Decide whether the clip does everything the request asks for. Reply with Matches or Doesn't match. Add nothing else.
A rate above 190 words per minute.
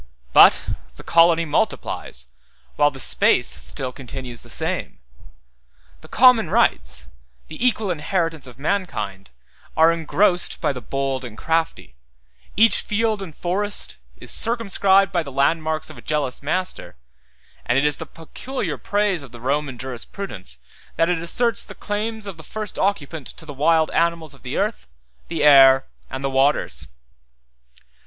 Doesn't match